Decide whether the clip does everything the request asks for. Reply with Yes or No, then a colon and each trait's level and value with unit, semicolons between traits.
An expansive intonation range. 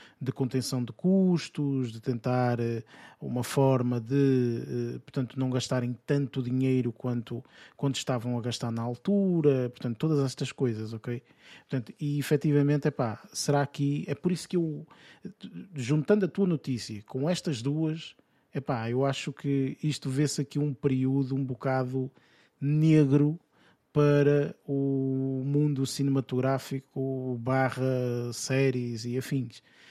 No: narrow, 2.4 semitones